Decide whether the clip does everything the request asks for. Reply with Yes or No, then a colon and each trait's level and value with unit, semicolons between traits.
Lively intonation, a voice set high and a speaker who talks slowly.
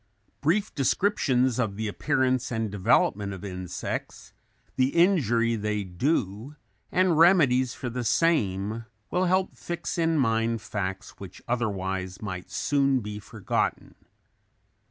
No: wide, 6.1 semitones; low, 115 Hz; slow, 120 wpm